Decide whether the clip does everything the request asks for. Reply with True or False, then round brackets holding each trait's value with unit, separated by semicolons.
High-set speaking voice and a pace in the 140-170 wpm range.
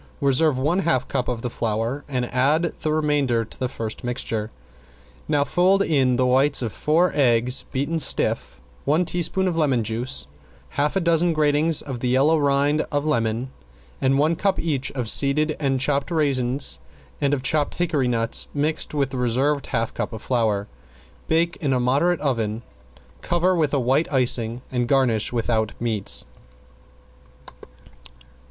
False (135 Hz; 160 wpm)